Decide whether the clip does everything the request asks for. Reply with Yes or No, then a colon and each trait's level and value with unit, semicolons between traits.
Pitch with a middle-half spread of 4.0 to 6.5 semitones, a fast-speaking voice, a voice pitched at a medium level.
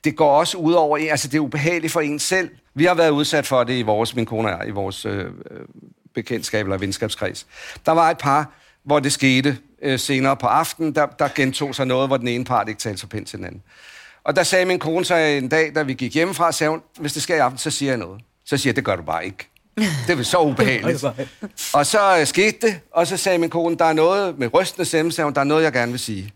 Yes: average, 4.8 semitones; fast, 265 wpm; medium, 145 Hz